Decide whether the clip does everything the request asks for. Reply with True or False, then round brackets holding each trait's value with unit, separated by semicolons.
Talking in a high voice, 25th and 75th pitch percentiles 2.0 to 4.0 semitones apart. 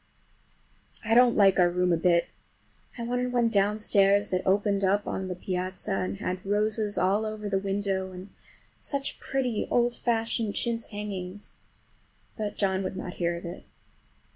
True (200 Hz; 2.9 semitones)